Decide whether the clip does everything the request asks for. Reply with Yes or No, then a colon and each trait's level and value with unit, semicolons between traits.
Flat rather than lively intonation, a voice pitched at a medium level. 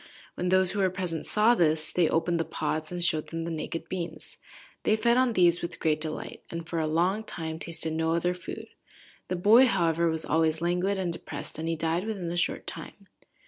Yes: narrow, 2.3 semitones; medium, 170 Hz